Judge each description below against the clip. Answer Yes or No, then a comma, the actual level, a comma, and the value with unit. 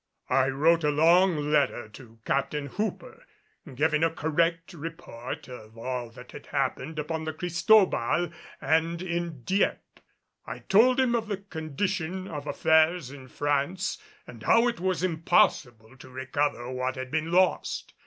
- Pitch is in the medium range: Yes, medium, 160 Hz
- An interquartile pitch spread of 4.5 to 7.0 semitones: Yes, average, 4.9 semitones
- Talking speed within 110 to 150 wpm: Yes, average, 145 wpm